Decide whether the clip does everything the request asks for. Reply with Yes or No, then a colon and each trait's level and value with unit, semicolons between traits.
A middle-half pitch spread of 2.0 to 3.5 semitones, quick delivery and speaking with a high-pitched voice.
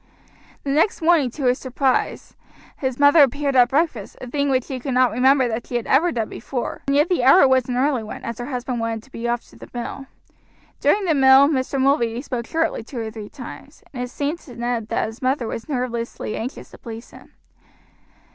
Yes: average, 3.0 semitones; fast, 220 wpm; very high, 255 Hz